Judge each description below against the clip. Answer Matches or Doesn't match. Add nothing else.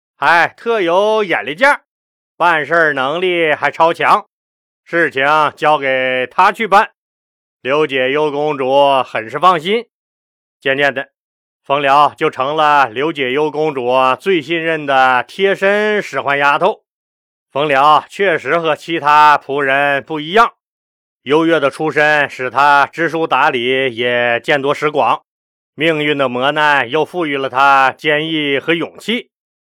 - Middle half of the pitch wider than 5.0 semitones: Doesn't match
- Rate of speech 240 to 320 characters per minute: Doesn't match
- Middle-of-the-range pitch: Matches